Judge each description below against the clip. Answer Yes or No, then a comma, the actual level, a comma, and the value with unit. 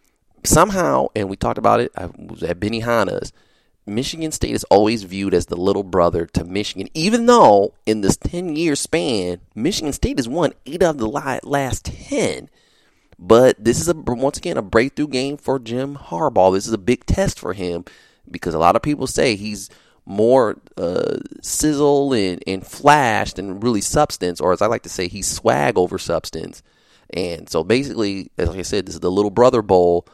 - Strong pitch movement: Yes, wide, 6.6 semitones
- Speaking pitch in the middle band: No, low, 110 Hz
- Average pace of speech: Yes, average, 190 wpm